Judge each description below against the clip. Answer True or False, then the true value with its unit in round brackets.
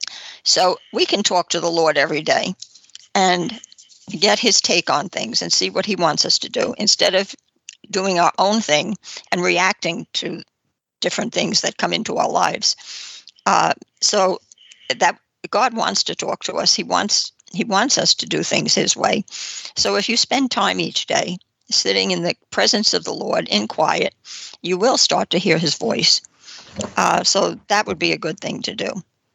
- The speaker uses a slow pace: False (185 wpm)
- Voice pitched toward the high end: True (195 Hz)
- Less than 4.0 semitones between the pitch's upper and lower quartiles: False (4.3 semitones)